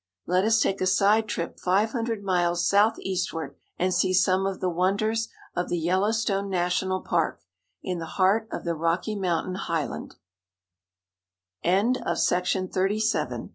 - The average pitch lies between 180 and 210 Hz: Yes, medium, 185 Hz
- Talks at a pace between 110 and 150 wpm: Yes, slow, 135 wpm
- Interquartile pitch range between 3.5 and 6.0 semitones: No, narrow, 2.5 semitones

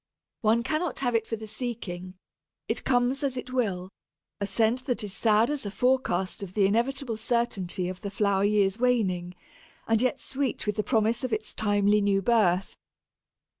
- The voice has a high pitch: Yes, high, 220 Hz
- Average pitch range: Yes, average, 3.7 semitones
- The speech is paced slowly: No, average, 175 wpm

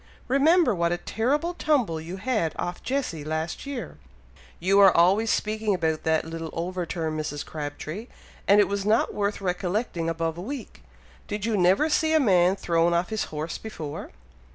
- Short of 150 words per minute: No, average, 170 wpm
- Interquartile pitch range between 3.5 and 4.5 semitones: No, average, 5.1 semitones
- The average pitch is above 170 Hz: Yes, medium, 185 Hz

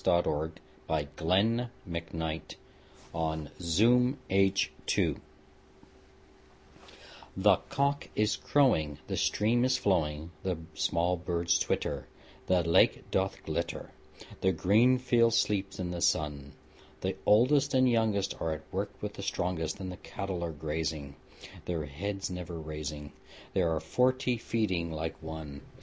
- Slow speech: Yes, slow, 120 wpm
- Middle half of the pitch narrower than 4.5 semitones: No, average, 5.1 semitones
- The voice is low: Yes, very low, 90 Hz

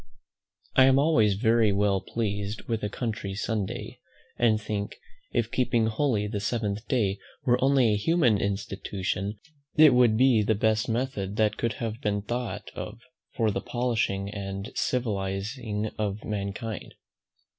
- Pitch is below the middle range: Yes, low, 110 Hz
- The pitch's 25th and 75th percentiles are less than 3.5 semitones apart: Yes, average, 2.8 semitones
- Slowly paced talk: No, average, 145 wpm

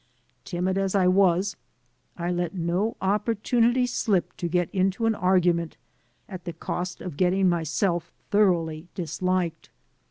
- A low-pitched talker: No, medium, 180 Hz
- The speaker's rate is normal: No, slow, 130 wpm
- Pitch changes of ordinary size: No, narrow, 2.2 semitones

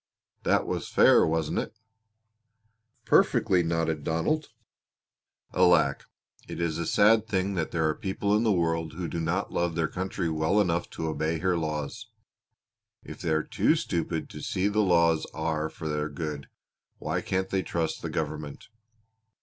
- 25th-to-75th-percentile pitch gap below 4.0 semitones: Yes, average, 2.9 semitones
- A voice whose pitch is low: Yes, very low, 85 Hz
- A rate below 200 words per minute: Yes, average, 160 wpm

